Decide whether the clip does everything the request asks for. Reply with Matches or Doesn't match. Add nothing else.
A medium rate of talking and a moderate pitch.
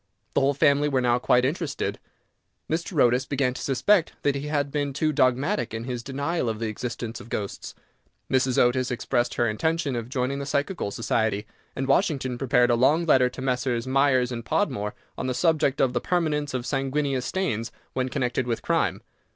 Doesn't match